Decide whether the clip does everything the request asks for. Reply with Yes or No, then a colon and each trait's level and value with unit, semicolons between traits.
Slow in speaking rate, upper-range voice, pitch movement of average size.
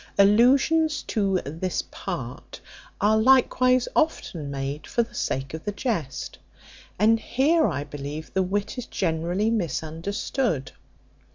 No: slow, 120 wpm; high, 200 Hz; wide, 7.4 semitones